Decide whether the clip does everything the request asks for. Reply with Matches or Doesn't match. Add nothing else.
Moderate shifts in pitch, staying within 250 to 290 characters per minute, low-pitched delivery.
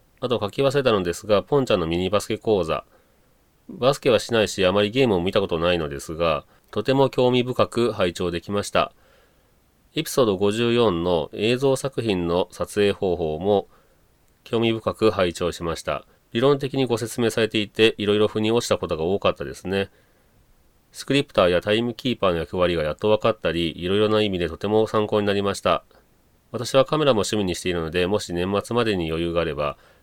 Doesn't match